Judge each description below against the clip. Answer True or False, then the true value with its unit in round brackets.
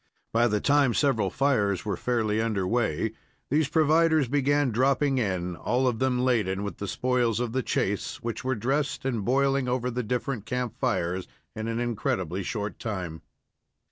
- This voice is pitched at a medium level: False (120 Hz)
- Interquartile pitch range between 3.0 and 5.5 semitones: True (4.2 semitones)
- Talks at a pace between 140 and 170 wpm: True (165 wpm)